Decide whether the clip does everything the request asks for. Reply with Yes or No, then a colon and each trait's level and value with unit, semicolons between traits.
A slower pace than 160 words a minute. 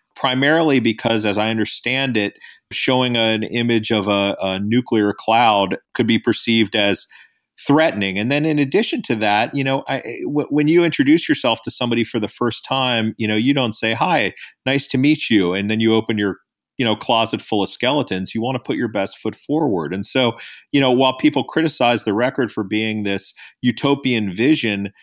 No: average, 195 wpm